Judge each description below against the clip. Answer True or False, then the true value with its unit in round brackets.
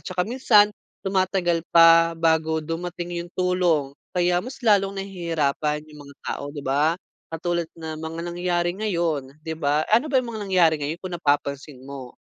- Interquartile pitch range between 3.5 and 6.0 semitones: False (2.8 semitones)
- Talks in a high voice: False (170 Hz)